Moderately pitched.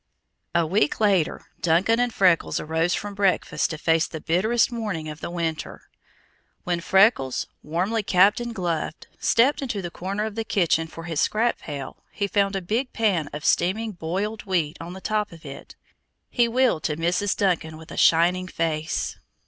Yes: medium, 180 Hz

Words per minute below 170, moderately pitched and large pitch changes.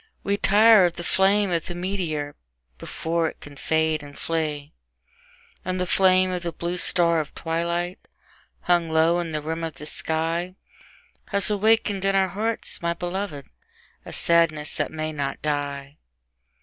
No: average, 160 wpm; medium, 170 Hz; average, 2.9 semitones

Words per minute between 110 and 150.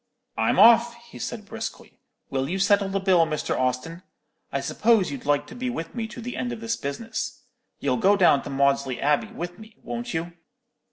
No: average, 200 wpm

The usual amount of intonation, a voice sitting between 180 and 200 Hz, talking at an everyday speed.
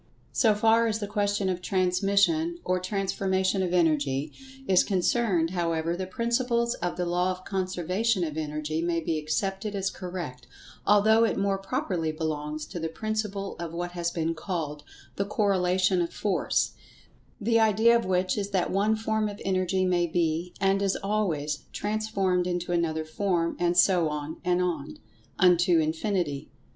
Yes: average, 3.2 semitones; medium, 185 Hz; average, 160 wpm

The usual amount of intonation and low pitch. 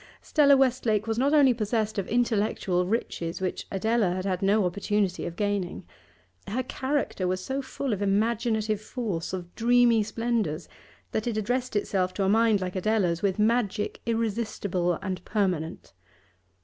No: average, 3.8 semitones; high, 210 Hz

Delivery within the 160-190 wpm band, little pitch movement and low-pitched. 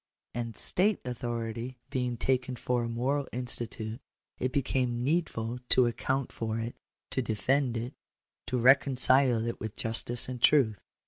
No: average, 140 wpm; narrow, 2.2 semitones; low, 125 Hz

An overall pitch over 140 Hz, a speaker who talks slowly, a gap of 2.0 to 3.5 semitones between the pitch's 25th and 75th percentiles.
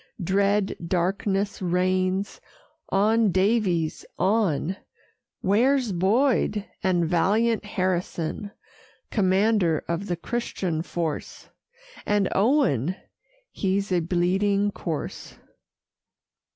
Yes: high, 190 Hz; slow, 80 wpm; average, 2.8 semitones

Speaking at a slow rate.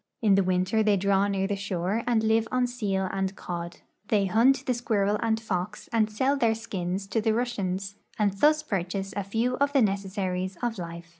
No: average, 200 wpm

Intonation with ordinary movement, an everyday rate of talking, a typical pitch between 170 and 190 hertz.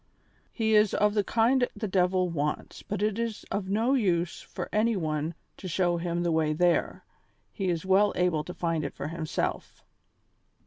Yes: average, 3.9 semitones; average, 180 wpm; medium, 185 Hz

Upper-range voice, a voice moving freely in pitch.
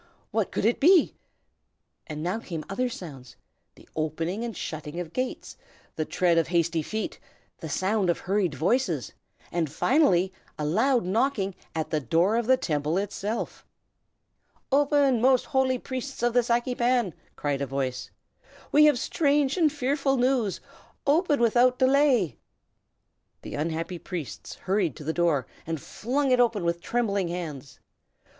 Yes: high, 205 Hz; wide, 7.6 semitones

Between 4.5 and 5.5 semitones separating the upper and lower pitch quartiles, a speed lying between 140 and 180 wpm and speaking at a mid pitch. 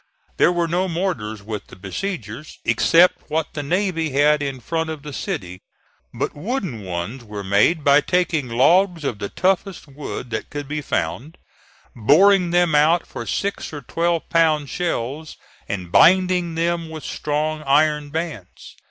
Yes: average, 5.1 semitones; average, 155 wpm; medium, 155 Hz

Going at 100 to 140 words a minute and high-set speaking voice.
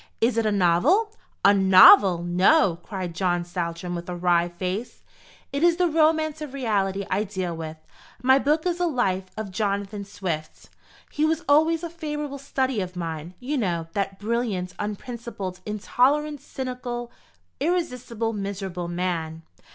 No: average, 150 wpm; high, 205 Hz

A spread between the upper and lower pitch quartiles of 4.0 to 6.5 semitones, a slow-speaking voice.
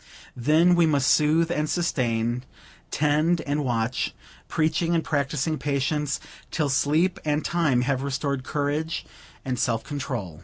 No: average, 3.2 semitones; slow, 130 wpm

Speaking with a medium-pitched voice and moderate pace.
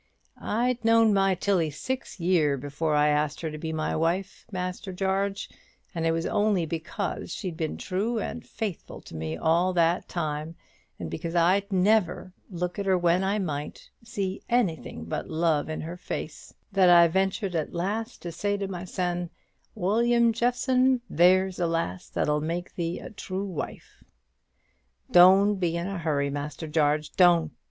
Yes: medium, 180 Hz; average, 165 wpm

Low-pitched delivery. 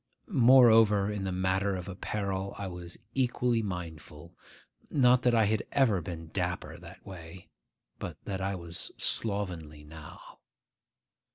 Yes: very low, 95 Hz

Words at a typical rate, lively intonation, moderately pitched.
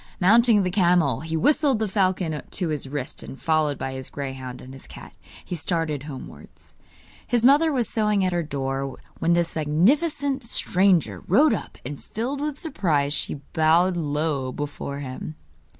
Yes: average, 165 wpm; wide, 6.8 semitones; medium, 165 Hz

